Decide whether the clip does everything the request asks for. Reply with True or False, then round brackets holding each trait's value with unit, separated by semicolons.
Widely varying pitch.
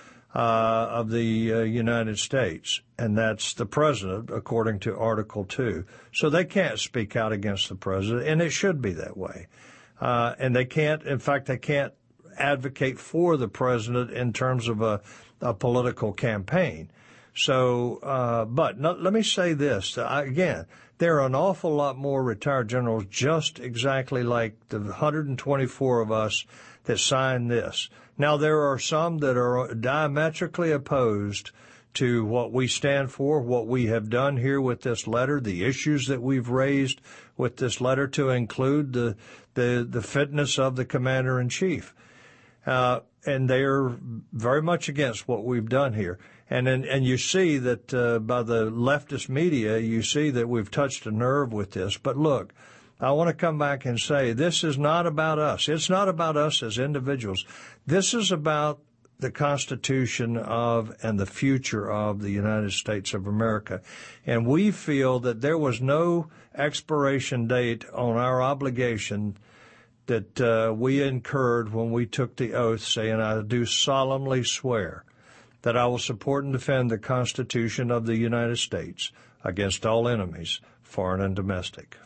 False (3.6 semitones)